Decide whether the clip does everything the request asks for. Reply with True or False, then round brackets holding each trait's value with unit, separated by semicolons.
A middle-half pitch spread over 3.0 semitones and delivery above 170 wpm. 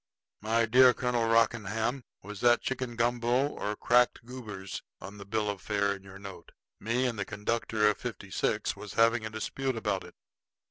False (2.7 semitones; 180 wpm)